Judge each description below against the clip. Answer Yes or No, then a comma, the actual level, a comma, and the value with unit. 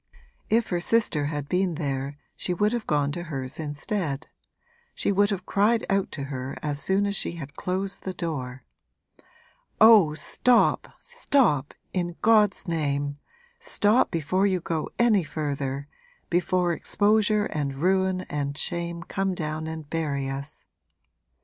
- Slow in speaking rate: No, average, 145 wpm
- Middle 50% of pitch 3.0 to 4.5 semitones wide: No, wide, 5.4 semitones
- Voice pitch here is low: No, medium, 170 Hz